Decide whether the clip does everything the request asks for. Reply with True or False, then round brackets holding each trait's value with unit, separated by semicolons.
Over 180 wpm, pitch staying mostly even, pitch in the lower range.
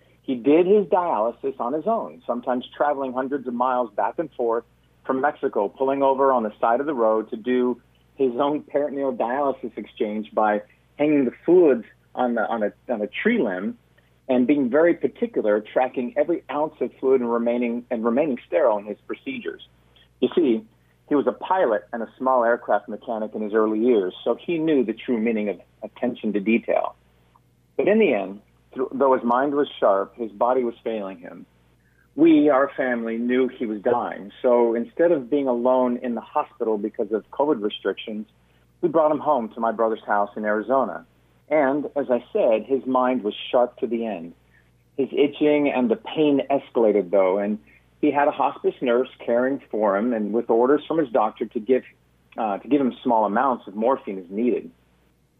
False (190 wpm; 4.4 semitones; 120 Hz)